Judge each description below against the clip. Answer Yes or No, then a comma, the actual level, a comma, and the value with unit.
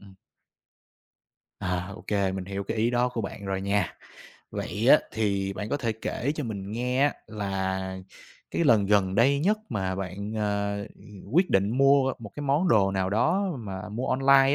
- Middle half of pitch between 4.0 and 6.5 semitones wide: Yes, average, 4.7 semitones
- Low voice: Yes, low, 105 Hz